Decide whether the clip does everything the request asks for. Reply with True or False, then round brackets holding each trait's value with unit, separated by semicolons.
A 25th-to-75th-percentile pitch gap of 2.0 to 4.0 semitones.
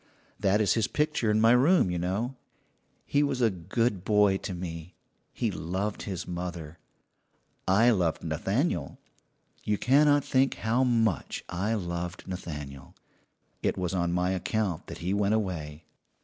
False (4.5 semitones)